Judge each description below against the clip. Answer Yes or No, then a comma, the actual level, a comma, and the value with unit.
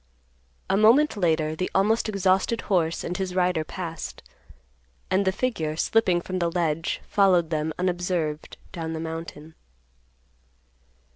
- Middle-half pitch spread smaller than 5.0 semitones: Yes, average, 3.1 semitones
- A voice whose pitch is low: No, medium, 180 Hz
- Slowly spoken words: Yes, slow, 130 wpm